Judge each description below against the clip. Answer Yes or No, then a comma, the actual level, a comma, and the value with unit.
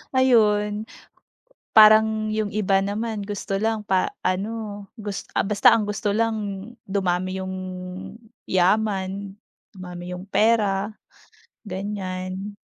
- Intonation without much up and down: Yes, narrow, 2.2 semitones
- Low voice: No, high, 205 Hz